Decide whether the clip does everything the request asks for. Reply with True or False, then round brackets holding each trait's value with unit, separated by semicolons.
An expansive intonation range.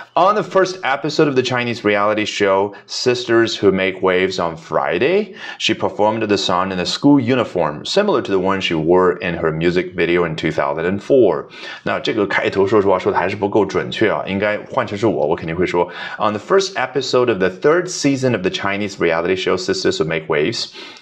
True (5.8 semitones)